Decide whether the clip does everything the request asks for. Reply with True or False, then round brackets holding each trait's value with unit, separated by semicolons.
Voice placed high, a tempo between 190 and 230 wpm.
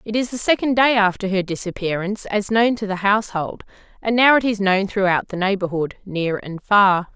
True (200 Hz; 200 wpm)